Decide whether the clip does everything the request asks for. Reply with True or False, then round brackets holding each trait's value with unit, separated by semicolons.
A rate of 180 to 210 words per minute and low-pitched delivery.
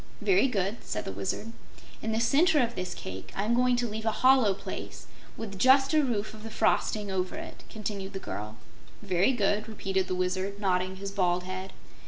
False (195 wpm; 205 Hz)